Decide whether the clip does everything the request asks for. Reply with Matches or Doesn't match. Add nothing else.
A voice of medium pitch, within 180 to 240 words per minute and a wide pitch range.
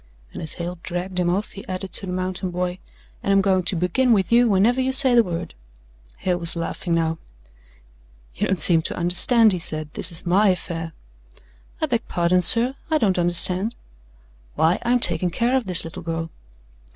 Doesn't match